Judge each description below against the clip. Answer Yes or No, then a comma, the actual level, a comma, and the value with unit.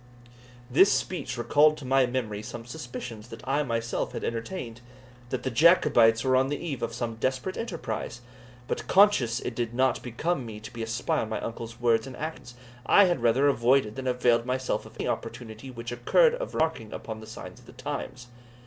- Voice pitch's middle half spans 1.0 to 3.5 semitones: Yes, average, 2.9 semitones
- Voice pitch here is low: Yes, low, 125 Hz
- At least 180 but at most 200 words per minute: Yes, average, 195 wpm